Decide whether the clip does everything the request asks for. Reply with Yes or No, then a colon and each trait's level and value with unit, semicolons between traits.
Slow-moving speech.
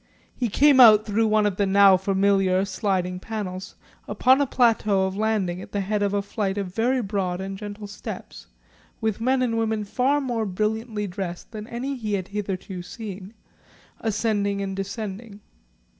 No: average, 170 wpm